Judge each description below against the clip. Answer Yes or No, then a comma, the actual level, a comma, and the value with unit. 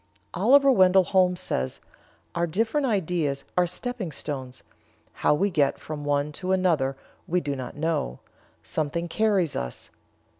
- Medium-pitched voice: Yes, medium, 170 Hz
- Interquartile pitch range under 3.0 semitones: No, average, 4.7 semitones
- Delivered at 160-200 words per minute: No, average, 140 wpm